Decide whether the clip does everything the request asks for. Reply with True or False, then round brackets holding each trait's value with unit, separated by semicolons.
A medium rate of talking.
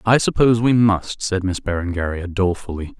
True (160 wpm)